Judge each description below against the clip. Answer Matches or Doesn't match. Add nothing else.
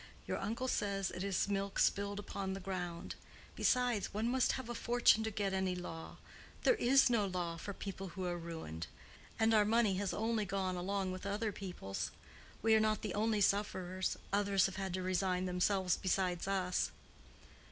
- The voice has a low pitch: Doesn't match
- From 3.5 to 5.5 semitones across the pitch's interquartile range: Doesn't match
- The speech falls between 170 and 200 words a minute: Matches